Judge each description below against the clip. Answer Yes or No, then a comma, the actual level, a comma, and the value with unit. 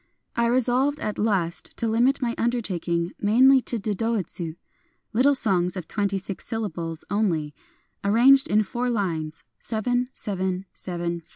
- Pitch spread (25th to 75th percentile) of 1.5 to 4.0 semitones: No, average, 5.1 semitones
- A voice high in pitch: Yes, high, 210 Hz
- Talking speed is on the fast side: No, average, 150 wpm